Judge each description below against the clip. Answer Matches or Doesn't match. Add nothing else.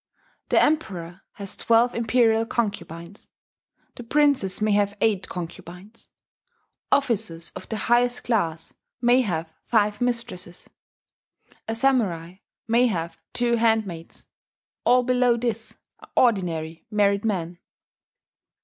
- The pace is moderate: Doesn't match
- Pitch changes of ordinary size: Matches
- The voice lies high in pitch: Matches